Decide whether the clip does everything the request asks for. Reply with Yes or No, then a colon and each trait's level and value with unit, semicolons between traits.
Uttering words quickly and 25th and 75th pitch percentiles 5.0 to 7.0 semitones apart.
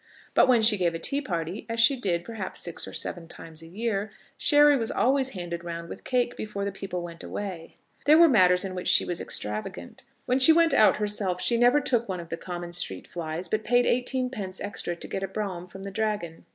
Yes: fast, 230 wpm; wide, 5.6 semitones